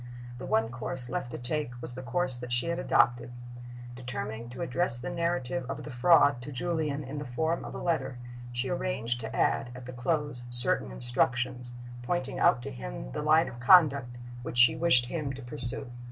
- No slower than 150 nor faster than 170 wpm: No, average, 195 wpm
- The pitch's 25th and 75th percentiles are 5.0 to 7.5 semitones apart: No, average, 3.4 semitones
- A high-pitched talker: No, low, 125 Hz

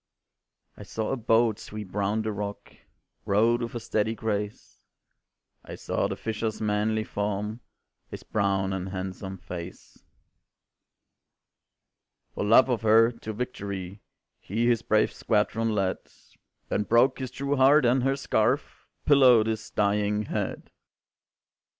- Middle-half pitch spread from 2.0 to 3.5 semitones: Yes, narrow, 2.5 semitones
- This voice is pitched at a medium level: No, low, 110 Hz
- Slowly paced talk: Yes, slow, 130 wpm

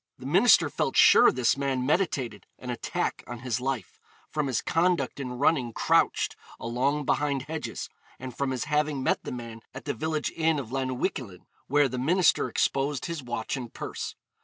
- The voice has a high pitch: No, low, 135 Hz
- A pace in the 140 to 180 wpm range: Yes, average, 175 wpm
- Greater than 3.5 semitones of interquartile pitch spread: No, average, 3.2 semitones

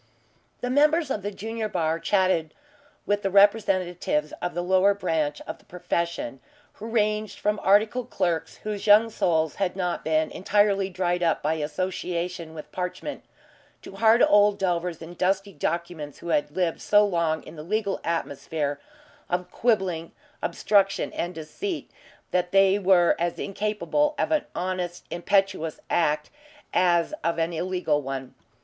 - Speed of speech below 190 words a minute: Yes, average, 150 wpm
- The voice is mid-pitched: Yes, medium, 180 Hz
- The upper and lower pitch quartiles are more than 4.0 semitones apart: No, average, 3.6 semitones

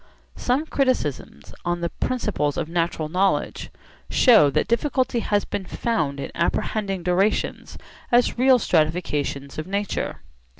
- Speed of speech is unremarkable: No, slow, 125 wpm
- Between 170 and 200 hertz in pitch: Yes, high, 190 Hz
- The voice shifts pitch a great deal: Yes, wide, 7.1 semitones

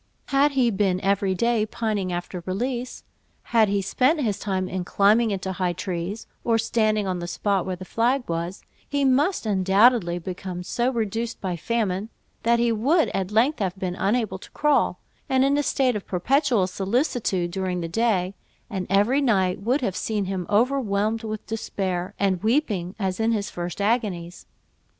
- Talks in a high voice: Yes, high, 205 Hz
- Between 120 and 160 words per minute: No, average, 175 wpm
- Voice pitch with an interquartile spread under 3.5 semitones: No, average, 4.1 semitones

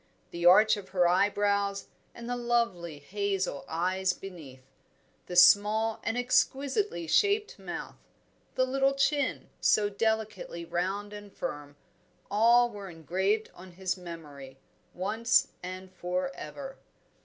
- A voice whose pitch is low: No, high, 200 Hz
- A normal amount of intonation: Yes, average, 4.1 semitones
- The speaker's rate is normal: No, slow, 120 wpm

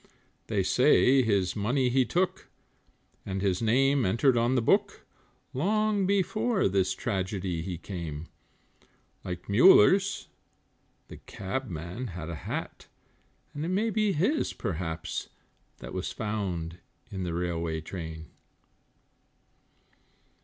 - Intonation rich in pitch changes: Yes, wide, 8.3 semitones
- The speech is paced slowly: Yes, slow, 115 wpm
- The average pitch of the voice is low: Yes, low, 105 Hz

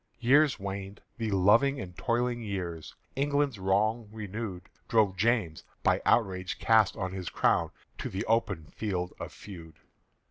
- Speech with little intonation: No, average, 3.8 semitones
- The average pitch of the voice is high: No, low, 105 Hz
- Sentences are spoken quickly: No, average, 145 wpm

